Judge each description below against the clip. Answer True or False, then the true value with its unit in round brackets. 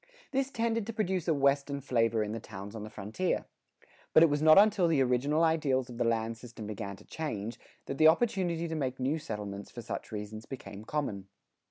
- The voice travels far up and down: True (6.6 semitones)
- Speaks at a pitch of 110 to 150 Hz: True (135 Hz)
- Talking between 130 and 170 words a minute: False (205 wpm)